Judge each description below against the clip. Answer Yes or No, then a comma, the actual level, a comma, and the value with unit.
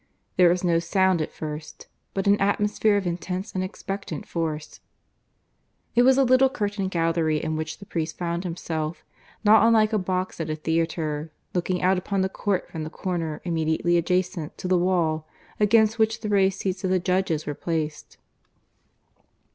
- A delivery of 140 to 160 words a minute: No, average, 170 wpm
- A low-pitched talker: No, medium, 180 Hz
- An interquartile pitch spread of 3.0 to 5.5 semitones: Yes, average, 3.6 semitones